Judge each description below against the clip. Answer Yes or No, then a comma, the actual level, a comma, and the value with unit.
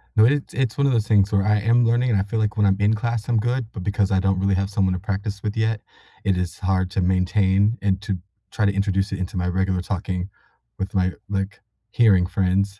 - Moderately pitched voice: No, low, 100 Hz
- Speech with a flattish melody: Yes, narrow, 2.3 semitones